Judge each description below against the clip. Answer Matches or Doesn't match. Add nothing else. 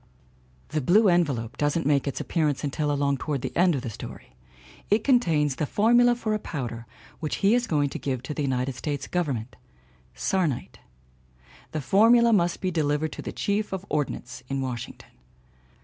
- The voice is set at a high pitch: Doesn't match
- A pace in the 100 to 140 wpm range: Doesn't match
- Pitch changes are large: Matches